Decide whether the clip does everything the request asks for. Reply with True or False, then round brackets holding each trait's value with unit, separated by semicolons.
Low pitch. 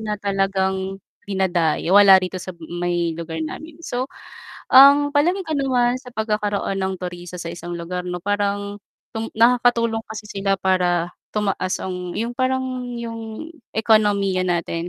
False (200 Hz)